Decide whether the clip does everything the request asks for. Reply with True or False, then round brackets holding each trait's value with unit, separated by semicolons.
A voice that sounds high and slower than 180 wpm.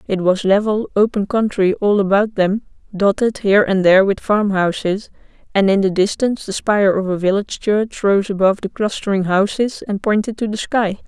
False (200 Hz; 185 wpm)